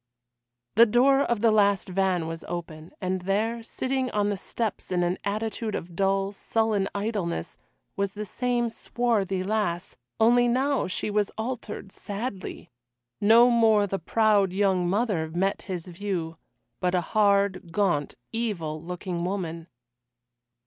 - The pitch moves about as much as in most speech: Yes, average, 3.7 semitones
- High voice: Yes, high, 200 Hz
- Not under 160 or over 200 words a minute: No, average, 140 wpm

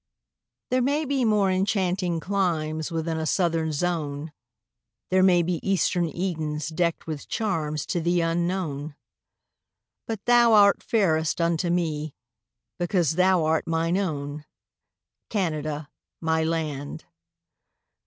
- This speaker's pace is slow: Yes, slow, 115 wpm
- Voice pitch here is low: No, medium, 170 Hz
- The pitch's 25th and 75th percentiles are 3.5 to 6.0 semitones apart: No, average, 3.1 semitones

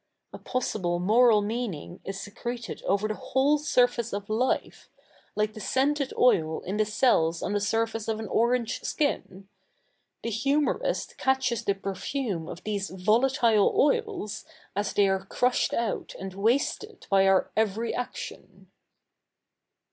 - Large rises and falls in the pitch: No, average, 4.0 semitones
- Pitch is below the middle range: No, high, 220 Hz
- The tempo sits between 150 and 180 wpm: No, average, 140 wpm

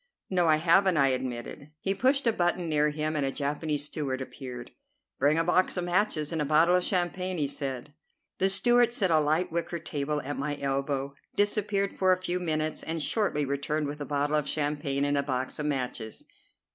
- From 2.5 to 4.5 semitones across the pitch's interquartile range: Yes, average, 4.1 semitones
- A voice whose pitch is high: No, medium, 155 Hz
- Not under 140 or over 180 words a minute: No, average, 200 wpm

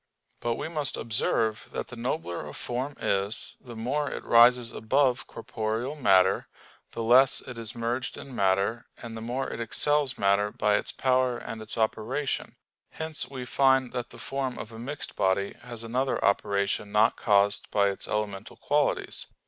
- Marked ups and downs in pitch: No, average, 3.3 semitones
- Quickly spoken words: No, average, 170 wpm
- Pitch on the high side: No, low, 115 Hz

